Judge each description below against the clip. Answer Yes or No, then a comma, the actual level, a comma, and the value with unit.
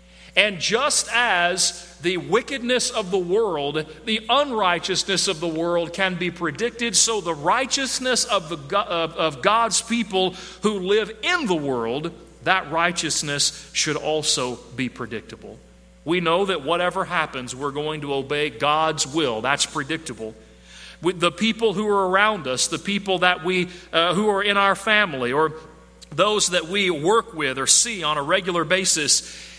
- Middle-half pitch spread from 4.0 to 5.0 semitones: Yes, average, 4.6 semitones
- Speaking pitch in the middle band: Yes, medium, 175 Hz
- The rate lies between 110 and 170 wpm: Yes, average, 160 wpm